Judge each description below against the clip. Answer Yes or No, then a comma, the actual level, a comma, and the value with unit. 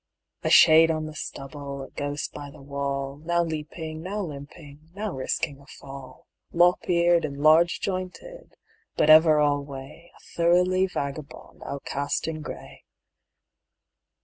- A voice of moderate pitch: Yes, medium, 155 Hz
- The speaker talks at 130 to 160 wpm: Yes, slow, 135 wpm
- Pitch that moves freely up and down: No, average, 3.4 semitones